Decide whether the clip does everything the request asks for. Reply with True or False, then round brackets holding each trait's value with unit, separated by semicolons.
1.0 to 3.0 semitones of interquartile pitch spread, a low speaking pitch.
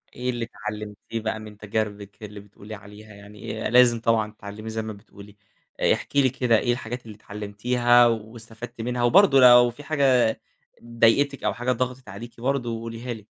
True (2.5 semitones; 115 Hz)